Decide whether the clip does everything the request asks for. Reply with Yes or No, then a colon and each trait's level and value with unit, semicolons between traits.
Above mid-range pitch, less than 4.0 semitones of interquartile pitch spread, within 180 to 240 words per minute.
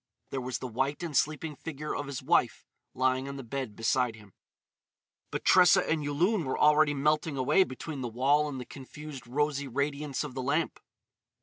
No: medium, 140 Hz; narrow, 2.6 semitones; average, 185 wpm